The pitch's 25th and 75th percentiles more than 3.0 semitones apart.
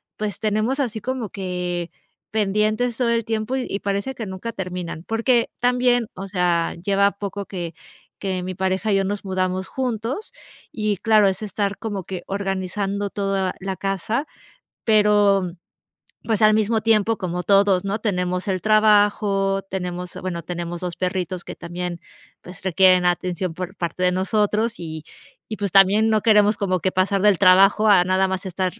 No: average, 2.7 semitones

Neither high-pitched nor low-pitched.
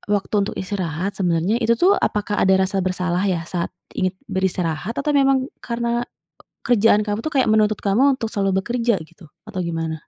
No: high, 200 Hz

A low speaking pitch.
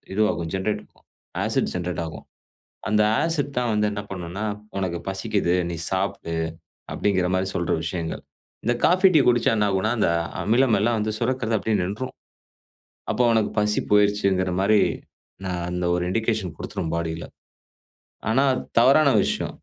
Yes: low, 105 Hz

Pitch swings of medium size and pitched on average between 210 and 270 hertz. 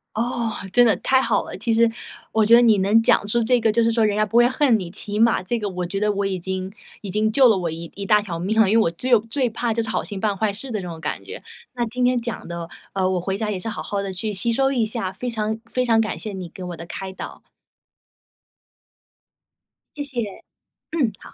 Yes: average, 3.4 semitones; high, 215 Hz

